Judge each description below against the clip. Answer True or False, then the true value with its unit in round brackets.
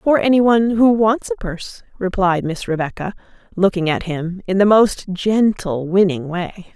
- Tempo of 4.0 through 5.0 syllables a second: True (4.7 syllables/s)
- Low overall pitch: False (195 Hz)